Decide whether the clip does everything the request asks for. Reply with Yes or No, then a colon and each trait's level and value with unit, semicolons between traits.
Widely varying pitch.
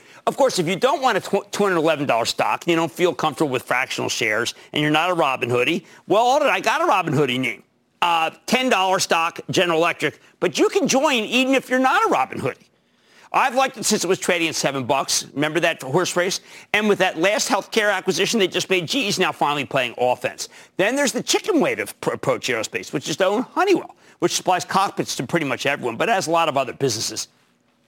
Yes: wide, 5.7 semitones